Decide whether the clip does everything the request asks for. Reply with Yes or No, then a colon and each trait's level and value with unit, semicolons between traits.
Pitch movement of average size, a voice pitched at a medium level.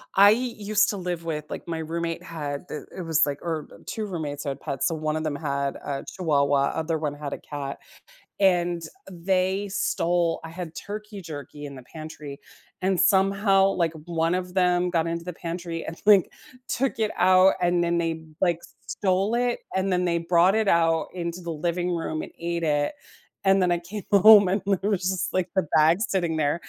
Yes: average, 3.0 semitones; medium, 170 Hz